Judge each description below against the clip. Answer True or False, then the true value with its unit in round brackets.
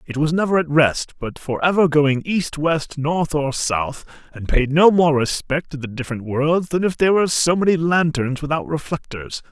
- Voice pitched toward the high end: False (155 Hz)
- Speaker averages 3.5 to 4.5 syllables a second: False (4.8 syllables/s)